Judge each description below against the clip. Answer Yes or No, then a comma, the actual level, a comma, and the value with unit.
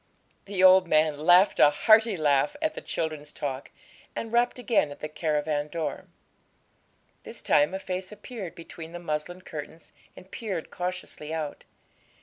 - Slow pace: No, average, 150 wpm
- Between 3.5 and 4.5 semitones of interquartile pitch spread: Yes, average, 3.9 semitones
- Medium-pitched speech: Yes, medium, 170 Hz